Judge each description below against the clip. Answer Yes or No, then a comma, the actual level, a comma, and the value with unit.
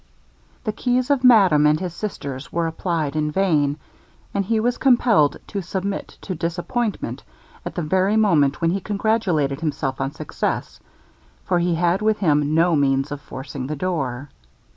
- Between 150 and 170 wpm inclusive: Yes, average, 165 wpm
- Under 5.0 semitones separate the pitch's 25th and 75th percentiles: No, wide, 5.4 semitones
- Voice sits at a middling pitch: Yes, medium, 170 Hz